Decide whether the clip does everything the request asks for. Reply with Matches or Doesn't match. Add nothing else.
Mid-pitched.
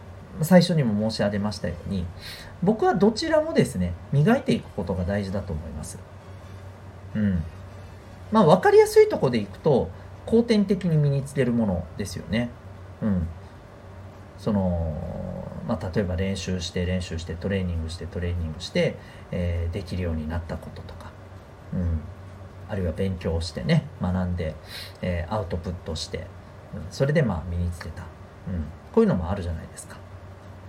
Doesn't match